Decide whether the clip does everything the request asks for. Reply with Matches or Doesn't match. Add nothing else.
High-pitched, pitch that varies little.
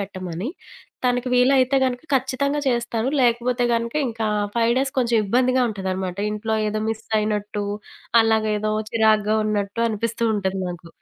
Doesn't match